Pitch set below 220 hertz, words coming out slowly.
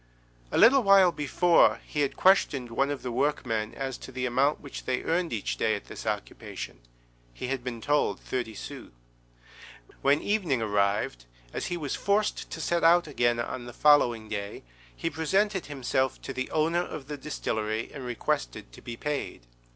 No: low, 135 Hz; average, 175 wpm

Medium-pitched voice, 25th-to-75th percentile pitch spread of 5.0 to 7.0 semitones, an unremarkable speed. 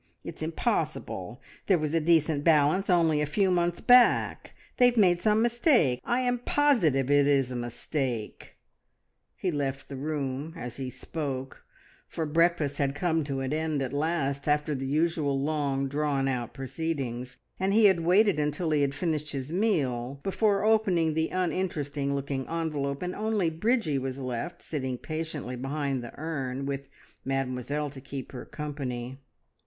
No: medium, 150 Hz; average, 4.0 semitones; average, 160 wpm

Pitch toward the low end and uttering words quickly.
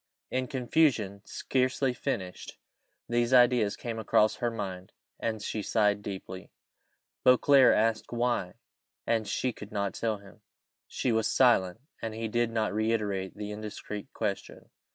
No: low, 110 Hz; slow, 135 wpm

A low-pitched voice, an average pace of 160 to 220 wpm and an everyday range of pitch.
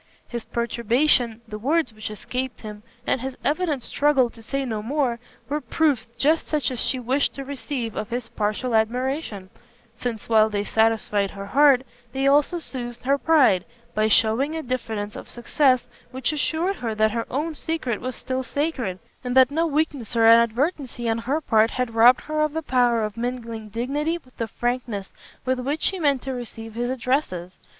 No: very high, 250 Hz; average, 180 wpm; average, 3.9 semitones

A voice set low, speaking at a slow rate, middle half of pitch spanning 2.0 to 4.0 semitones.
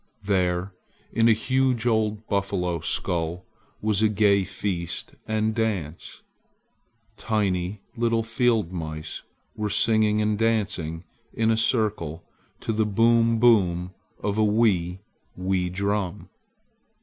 Yes: low, 105 Hz; slow, 115 wpm; average, 3.6 semitones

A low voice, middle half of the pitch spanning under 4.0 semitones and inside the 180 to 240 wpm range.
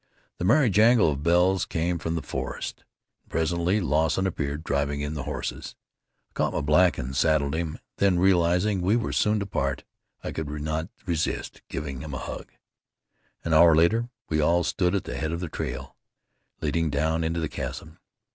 Yes: very low, 80 Hz; average, 3.0 semitones; average, 185 wpm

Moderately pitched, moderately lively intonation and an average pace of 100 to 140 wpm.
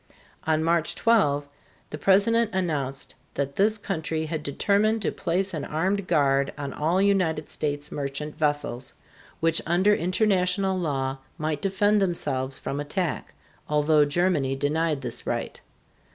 Yes: medium, 160 Hz; average, 4.7 semitones; slow, 135 wpm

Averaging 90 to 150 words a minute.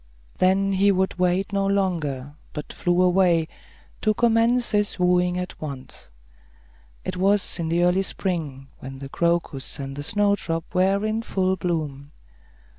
Yes: average, 145 wpm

